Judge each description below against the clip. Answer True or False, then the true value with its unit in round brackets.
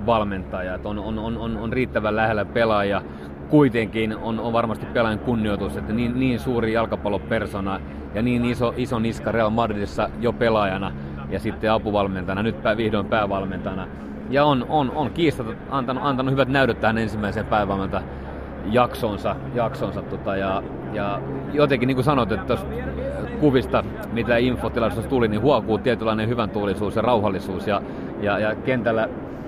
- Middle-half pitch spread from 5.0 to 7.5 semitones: False (3.4 semitones)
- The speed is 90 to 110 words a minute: False (145 wpm)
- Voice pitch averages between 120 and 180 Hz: False (110 Hz)